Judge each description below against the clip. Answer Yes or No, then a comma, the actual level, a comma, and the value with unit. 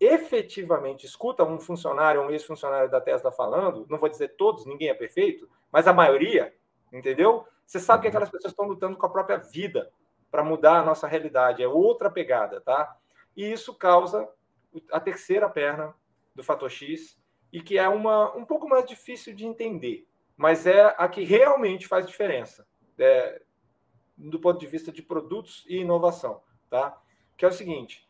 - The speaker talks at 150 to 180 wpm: Yes, average, 170 wpm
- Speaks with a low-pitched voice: No, high, 195 Hz